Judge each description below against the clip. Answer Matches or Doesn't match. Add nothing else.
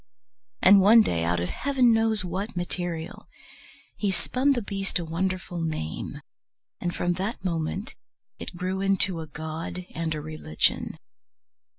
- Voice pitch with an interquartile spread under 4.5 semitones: Matches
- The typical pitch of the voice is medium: Matches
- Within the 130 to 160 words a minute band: Matches